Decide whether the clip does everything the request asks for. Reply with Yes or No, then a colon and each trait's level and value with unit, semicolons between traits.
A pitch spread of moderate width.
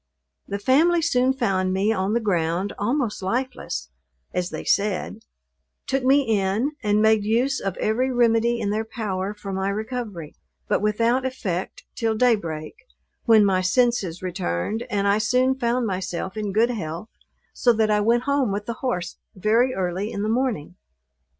Yes: average, 4.0 semitones